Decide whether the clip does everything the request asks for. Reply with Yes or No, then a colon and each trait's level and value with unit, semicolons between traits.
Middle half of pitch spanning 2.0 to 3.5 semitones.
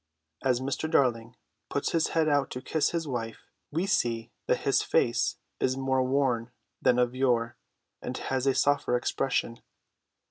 Yes: average, 2.7 semitones